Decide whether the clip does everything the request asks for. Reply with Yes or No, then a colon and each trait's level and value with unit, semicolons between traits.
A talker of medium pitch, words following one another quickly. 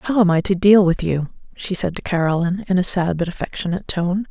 Yes: medium, 180 Hz; fast, 235 wpm